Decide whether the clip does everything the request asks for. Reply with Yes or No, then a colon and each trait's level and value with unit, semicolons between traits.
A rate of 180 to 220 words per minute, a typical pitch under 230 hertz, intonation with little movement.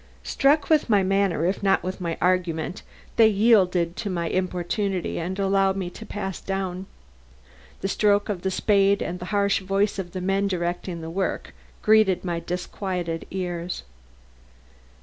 No: average, 155 wpm; high, 190 Hz; narrow, 2.1 semitones